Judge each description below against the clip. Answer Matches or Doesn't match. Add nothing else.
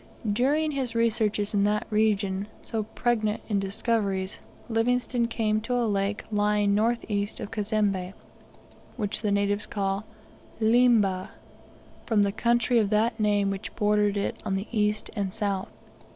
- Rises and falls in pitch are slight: Matches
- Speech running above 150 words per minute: Doesn't match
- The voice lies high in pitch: Matches